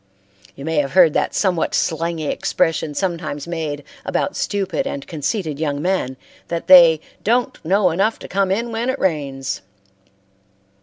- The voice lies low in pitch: No, medium, 170 Hz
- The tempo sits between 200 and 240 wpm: No, average, 150 wpm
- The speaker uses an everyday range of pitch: Yes, average, 4.4 semitones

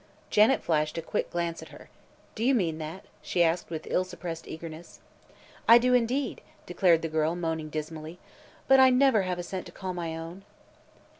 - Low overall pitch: No, medium, 175 Hz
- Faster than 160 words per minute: Yes, average, 190 wpm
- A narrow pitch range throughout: No, average, 4.3 semitones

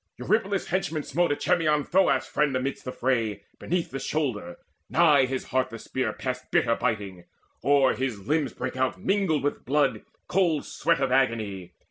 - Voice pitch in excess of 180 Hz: No, low, 135 Hz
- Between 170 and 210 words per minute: No, average, 160 wpm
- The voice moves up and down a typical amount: Yes, average, 3.9 semitones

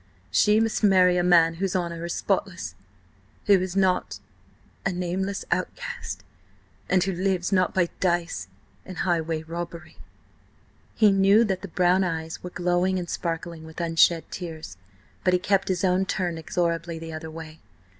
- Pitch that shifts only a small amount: Yes, narrow, 2.2 semitones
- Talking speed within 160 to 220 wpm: No, average, 145 wpm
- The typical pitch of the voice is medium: Yes, medium, 175 Hz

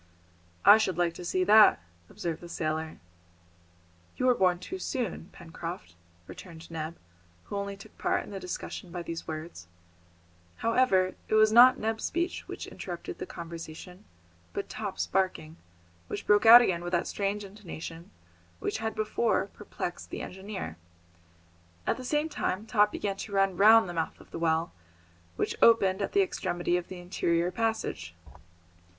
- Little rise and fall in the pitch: No, average, 4.2 semitones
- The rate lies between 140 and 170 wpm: Yes, average, 160 wpm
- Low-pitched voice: No, high, 190 Hz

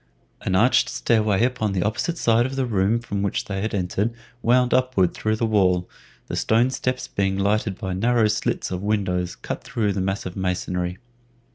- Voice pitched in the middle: No, low, 105 Hz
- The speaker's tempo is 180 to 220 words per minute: Yes, average, 185 wpm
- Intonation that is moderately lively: Yes, average, 3.6 semitones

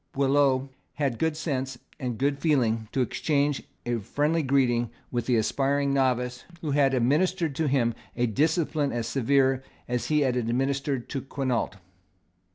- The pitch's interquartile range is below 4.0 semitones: Yes, average, 2.7 semitones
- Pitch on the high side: No, low, 135 Hz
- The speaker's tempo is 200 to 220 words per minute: No, average, 155 wpm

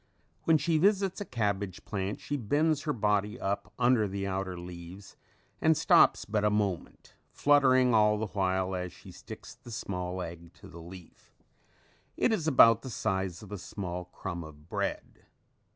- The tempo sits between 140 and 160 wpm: No, average, 170 wpm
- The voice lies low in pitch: Yes, low, 105 Hz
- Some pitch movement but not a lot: No, wide, 5.7 semitones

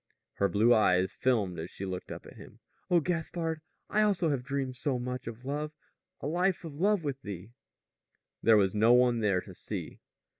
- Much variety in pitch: Yes, wide, 7.0 semitones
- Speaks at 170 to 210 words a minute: Yes, average, 190 wpm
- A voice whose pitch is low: Yes, low, 125 Hz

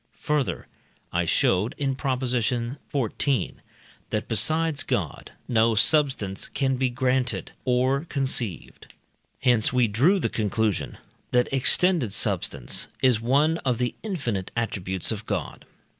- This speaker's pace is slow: Yes, slow, 120 wpm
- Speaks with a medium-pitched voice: No, low, 125 Hz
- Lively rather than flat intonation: No, average, 3.8 semitones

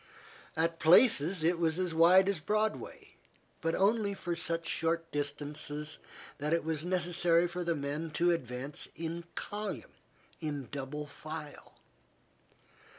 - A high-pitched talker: No, medium, 165 Hz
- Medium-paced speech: No, slow, 130 wpm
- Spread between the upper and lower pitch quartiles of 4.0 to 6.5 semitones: No, average, 2.7 semitones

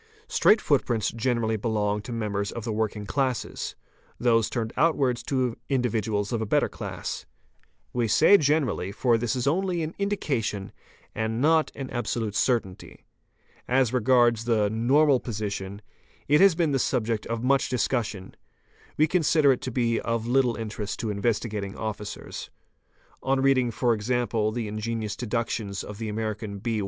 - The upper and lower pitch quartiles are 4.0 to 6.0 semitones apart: No, average, 3.4 semitones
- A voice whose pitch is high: No, low, 115 Hz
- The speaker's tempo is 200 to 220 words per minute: No, average, 150 wpm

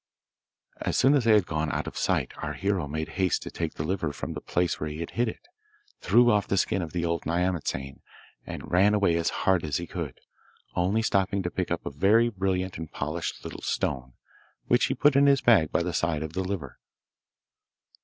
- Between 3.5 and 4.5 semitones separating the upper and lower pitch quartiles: Yes, average, 4.1 semitones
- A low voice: Yes, very low, 90 Hz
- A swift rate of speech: Yes, fast, 215 wpm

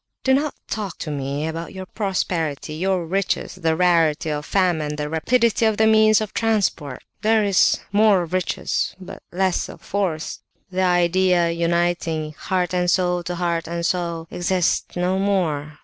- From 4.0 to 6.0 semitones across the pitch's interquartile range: No, average, 2.9 semitones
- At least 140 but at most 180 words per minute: Yes, average, 160 wpm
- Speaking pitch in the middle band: Yes, medium, 180 Hz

